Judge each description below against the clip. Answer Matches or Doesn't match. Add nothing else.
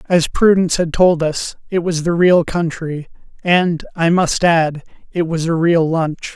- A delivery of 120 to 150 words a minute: Doesn't match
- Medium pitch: Matches